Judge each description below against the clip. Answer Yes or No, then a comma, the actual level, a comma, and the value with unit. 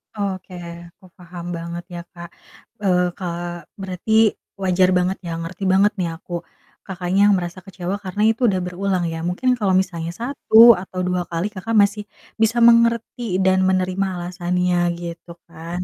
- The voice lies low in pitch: No, medium, 185 Hz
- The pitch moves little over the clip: Yes, narrow, 2.1 semitones